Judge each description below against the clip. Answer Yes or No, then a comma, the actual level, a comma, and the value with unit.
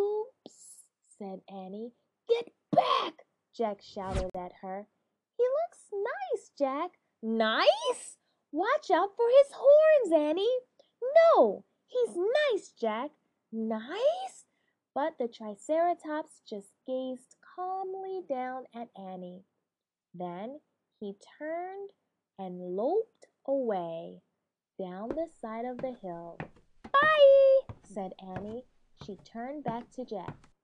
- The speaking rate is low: Yes, slow, 105 wpm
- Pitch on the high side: Yes, very high, 260 Hz